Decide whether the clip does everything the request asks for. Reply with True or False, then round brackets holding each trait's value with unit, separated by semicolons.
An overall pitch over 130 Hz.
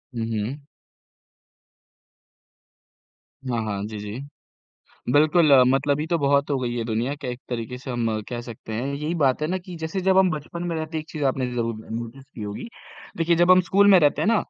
True (140 Hz)